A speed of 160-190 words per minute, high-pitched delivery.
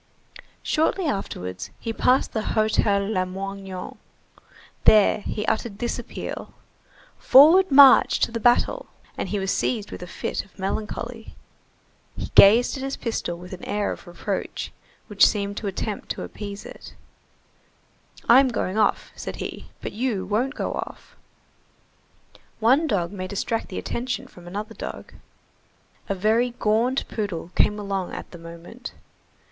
No: average, 145 wpm; high, 210 Hz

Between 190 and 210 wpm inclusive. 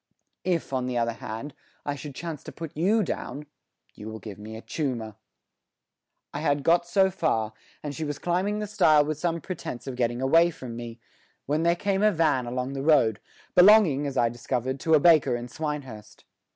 Yes: average, 195 wpm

